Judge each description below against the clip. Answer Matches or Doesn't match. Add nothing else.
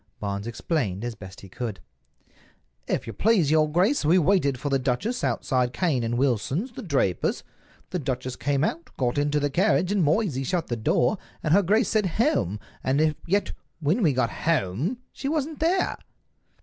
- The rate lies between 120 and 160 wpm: Doesn't match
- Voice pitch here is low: Doesn't match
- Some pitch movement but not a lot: Doesn't match